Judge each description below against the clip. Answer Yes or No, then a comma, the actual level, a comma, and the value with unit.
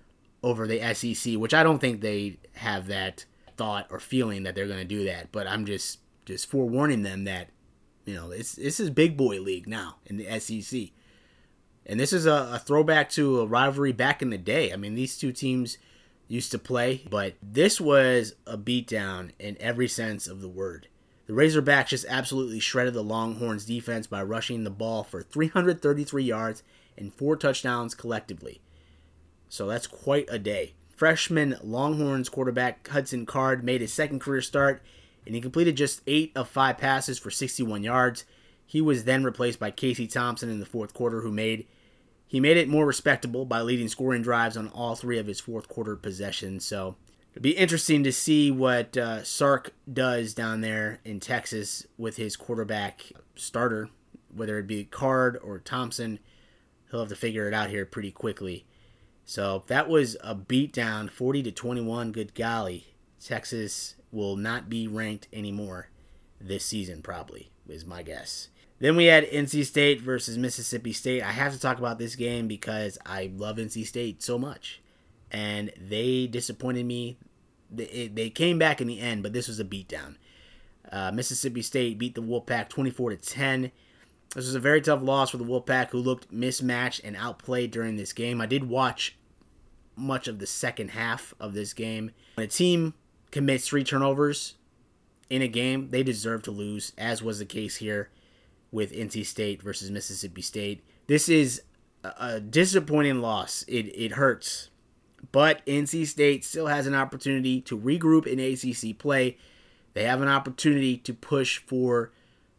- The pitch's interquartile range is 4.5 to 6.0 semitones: No, average, 3.8 semitones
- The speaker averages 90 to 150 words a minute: No, average, 175 wpm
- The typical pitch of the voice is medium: No, low, 120 Hz